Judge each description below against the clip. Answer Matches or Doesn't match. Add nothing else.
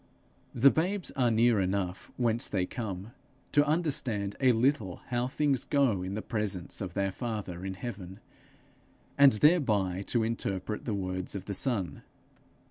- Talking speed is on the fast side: Doesn't match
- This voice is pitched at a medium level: Doesn't match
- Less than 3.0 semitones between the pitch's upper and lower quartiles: Doesn't match